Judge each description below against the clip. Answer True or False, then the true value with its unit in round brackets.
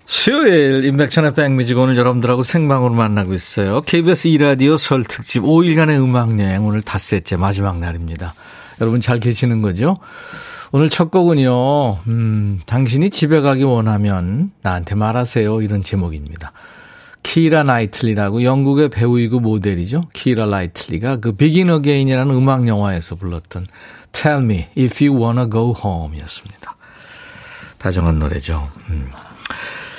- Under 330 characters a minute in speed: False (350 characters per minute)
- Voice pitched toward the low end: True (120 Hz)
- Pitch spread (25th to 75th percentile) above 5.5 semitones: True (6.2 semitones)